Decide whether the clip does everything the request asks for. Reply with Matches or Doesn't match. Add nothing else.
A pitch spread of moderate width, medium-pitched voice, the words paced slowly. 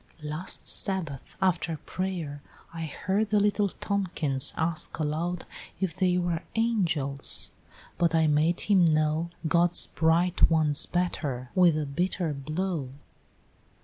Matches